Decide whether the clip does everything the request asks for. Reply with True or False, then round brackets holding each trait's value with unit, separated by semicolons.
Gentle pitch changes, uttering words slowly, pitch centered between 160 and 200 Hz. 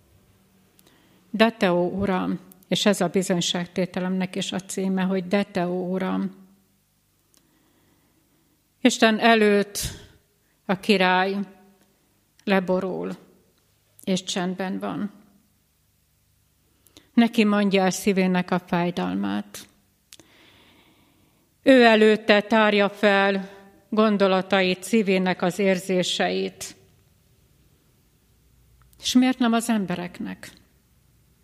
True (2.3 semitones; 75 wpm; 190 Hz)